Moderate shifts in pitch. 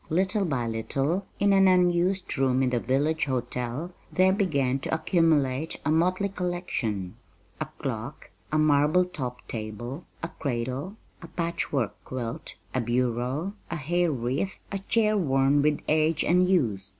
No: wide, 5.9 semitones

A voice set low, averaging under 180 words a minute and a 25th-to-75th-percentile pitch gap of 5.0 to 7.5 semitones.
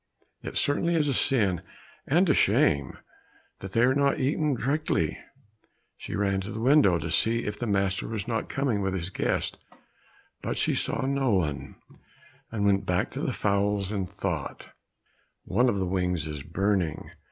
Yes: low, 100 Hz; average, 170 wpm; wide, 5.5 semitones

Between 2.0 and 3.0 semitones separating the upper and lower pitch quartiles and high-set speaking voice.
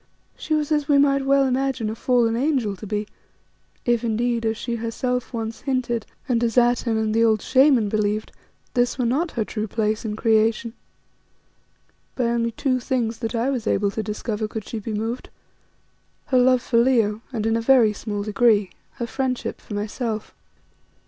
Yes: narrow, 2.6 semitones; high, 230 Hz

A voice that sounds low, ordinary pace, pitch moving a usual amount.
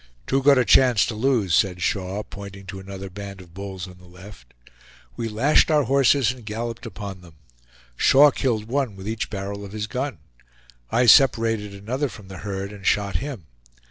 Yes: low, 105 Hz; average, 185 wpm; average, 4.2 semitones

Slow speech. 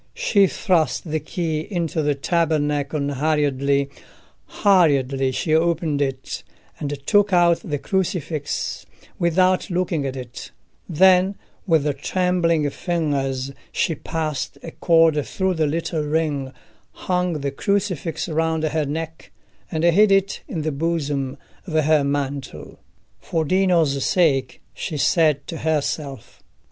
Yes: slow, 125 wpm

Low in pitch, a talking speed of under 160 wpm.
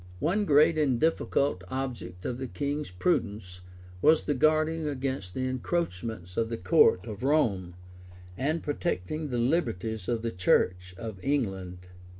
Yes: low, 120 Hz; average, 150 wpm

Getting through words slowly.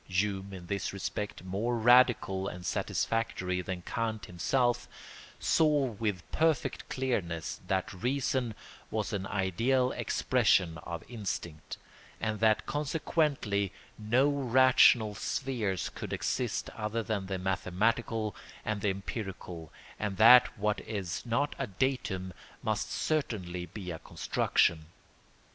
Yes: slow, 115 wpm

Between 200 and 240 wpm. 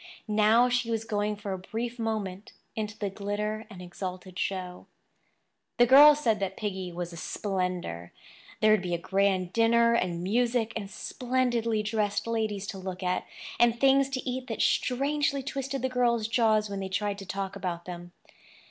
No: average, 175 wpm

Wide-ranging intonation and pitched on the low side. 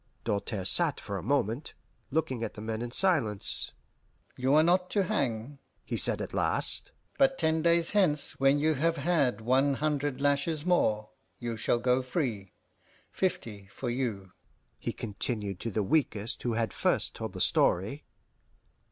Yes: wide, 6.1 semitones; low, 130 Hz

